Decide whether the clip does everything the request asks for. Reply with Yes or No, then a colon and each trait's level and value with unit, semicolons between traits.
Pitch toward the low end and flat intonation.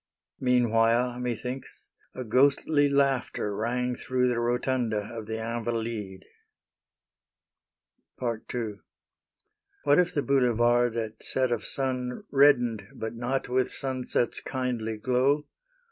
Yes: low, 125 Hz; narrow, 2.3 semitones